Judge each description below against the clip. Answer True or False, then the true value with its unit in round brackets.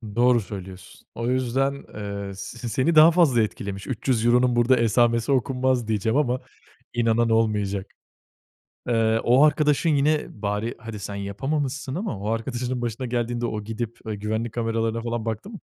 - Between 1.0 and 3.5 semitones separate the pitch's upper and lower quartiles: True (2.9 semitones)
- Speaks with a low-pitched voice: True (115 Hz)